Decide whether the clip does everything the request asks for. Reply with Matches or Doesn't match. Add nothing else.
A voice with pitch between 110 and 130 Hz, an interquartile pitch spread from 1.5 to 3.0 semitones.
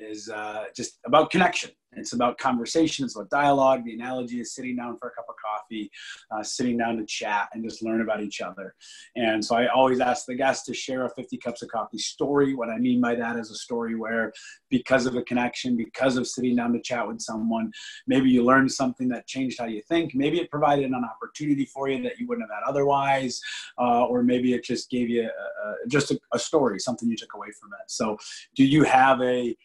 Matches